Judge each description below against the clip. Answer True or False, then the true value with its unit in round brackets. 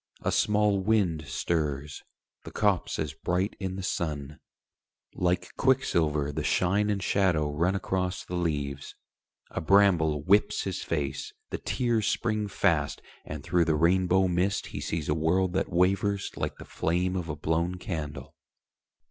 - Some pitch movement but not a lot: True (3.8 semitones)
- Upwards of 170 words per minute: False (150 wpm)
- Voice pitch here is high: False (90 Hz)